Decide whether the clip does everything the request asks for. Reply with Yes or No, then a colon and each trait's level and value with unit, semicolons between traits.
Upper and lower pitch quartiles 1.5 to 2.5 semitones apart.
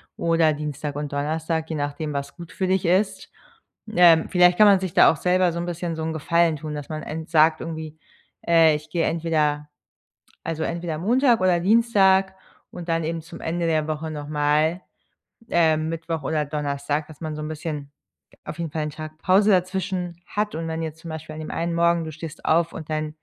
Yes: narrow, 2.0 semitones